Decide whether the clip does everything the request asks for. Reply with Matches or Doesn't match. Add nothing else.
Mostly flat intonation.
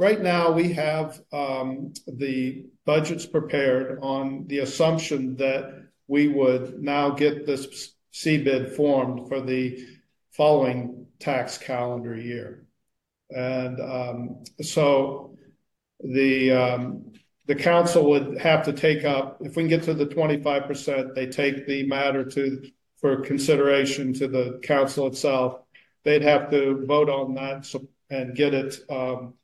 Matches